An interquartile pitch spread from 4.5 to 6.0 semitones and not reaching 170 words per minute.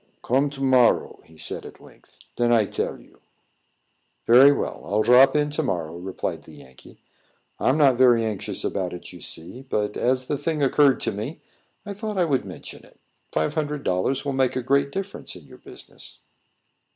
No: average, 5.1 semitones; average, 190 wpm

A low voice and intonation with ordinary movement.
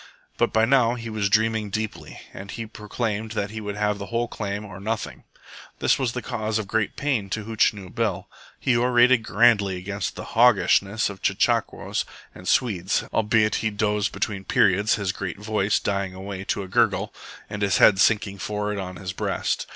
No: low, 105 Hz; narrow, 2.1 semitones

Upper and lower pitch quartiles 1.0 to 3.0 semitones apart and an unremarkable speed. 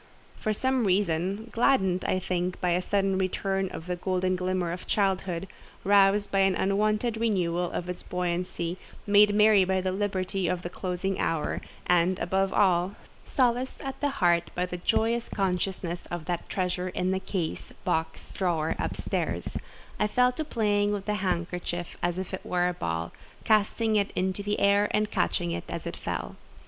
Yes: narrow, 2.5 semitones; average, 165 wpm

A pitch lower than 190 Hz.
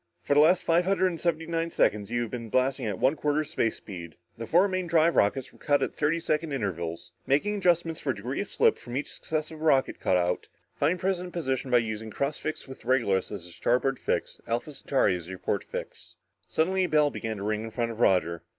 Yes: low, 135 Hz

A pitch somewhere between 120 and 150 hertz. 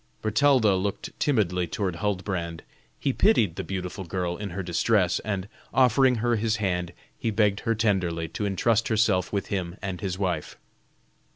No: low, 100 Hz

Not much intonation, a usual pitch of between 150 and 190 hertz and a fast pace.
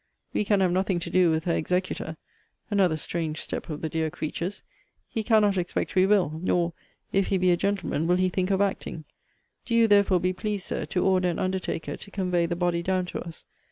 Yes: narrow, 2.3 semitones; medium, 185 Hz; fast, 215 wpm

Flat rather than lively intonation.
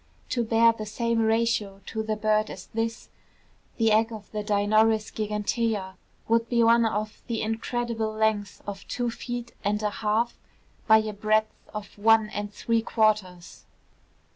Yes: narrow, 1.4 semitones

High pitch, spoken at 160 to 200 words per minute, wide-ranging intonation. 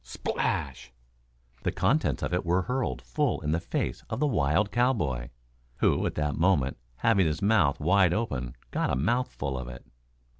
No: very low, 85 Hz; average, 165 wpm; wide, 8.5 semitones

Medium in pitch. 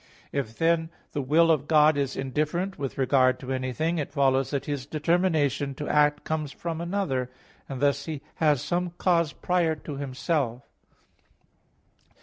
Yes: medium, 150 Hz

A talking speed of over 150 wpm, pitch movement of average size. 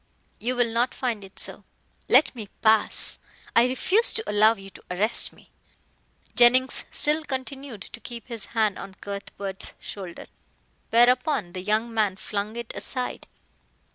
No: average, 145 wpm; average, 3.7 semitones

